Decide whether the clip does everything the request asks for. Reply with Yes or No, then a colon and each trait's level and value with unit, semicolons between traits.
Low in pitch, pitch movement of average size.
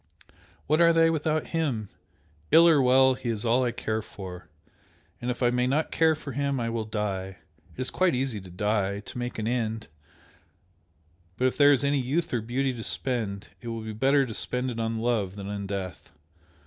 Yes: low, 120 Hz; average, 4.0 semitones